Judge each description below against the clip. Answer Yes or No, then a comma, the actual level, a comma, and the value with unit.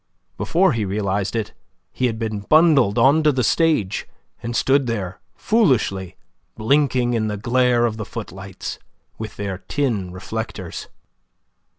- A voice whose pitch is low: Yes, low, 115 Hz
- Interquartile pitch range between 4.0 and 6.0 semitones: Yes, average, 4.8 semitones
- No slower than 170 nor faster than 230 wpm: No, slow, 135 wpm